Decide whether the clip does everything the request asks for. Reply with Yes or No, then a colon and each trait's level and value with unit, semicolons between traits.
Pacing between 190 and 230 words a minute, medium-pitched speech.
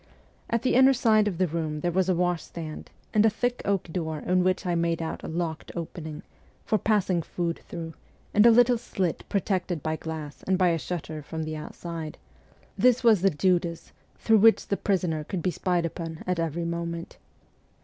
Yes: average, 195 wpm; medium, 175 Hz